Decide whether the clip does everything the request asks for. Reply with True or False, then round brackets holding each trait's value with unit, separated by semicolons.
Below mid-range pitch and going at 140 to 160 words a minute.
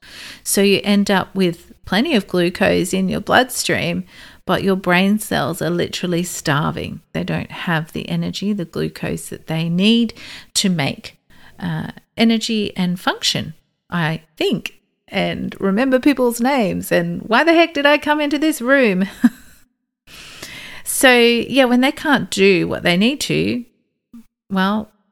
False (200 Hz; 145 wpm)